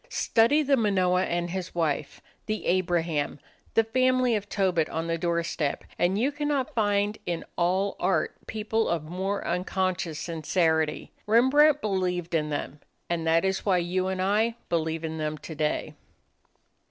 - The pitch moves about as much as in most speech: Yes, average, 4.3 semitones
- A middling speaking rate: Yes, average, 150 wpm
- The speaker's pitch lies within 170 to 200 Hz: Yes, medium, 185 Hz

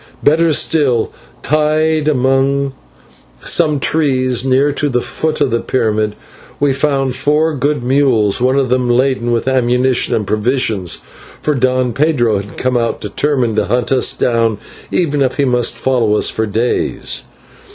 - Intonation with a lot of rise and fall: No, average, 3.2 semitones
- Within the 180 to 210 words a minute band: No, average, 150 wpm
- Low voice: Yes, low, 130 Hz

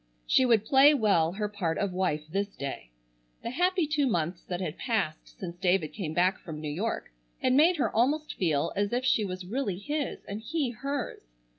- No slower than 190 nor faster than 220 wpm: Yes, average, 195 wpm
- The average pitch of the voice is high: Yes, high, 205 Hz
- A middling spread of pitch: No, wide, 6.8 semitones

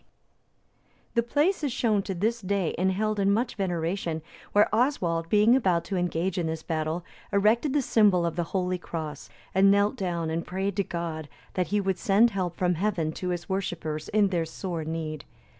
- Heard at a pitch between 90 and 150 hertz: No, medium, 185 Hz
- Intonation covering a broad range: No, average, 3.6 semitones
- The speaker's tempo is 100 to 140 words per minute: No, average, 190 wpm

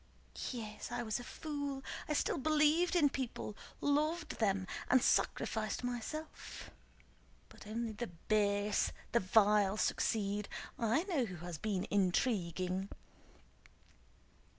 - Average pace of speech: No, slow, 115 wpm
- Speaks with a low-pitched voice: No, high, 220 Hz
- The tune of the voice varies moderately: No, wide, 5.7 semitones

